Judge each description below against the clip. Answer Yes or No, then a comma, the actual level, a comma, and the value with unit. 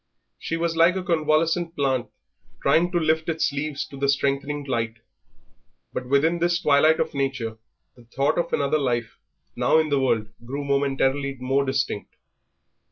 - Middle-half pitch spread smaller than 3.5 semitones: Yes, average, 3.1 semitones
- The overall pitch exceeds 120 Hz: Yes, medium, 140 Hz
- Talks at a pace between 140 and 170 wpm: Yes, average, 160 wpm